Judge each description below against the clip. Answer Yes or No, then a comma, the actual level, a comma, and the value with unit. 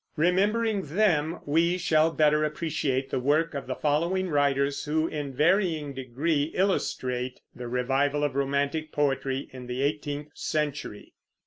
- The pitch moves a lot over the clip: No, average, 2.9 semitones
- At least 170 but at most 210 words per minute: No, slow, 135 wpm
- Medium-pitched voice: Yes, medium, 150 Hz